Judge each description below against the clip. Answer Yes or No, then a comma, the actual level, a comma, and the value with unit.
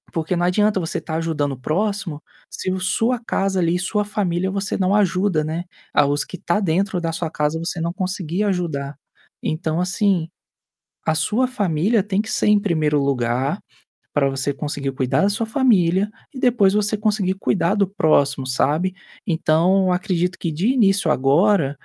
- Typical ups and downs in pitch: Yes, average, 4.4 semitones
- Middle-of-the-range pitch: Yes, medium, 180 Hz